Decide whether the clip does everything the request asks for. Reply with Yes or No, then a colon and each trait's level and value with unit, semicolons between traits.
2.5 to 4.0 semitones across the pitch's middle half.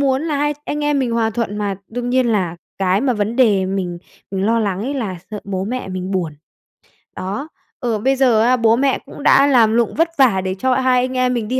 No: average, 4.7 semitones